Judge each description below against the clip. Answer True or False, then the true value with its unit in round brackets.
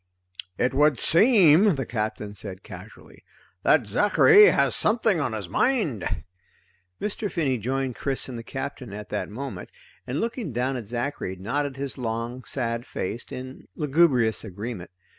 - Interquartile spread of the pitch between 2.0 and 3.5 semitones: False (5.0 semitones)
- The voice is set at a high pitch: False (130 Hz)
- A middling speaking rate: True (145 wpm)